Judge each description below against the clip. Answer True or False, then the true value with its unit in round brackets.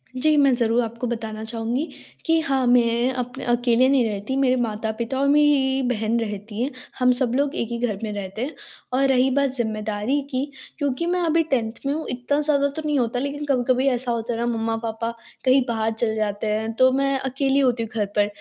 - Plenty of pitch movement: False (3.2 semitones)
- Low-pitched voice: False (245 Hz)